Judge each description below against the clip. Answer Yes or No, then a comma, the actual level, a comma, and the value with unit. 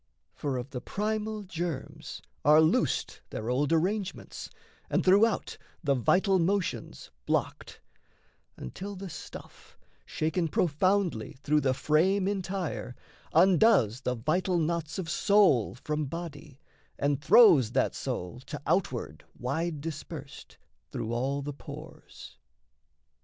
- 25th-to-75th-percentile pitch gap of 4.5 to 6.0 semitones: Yes, wide, 5.4 semitones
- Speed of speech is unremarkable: No, slow, 115 wpm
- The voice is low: No, medium, 160 Hz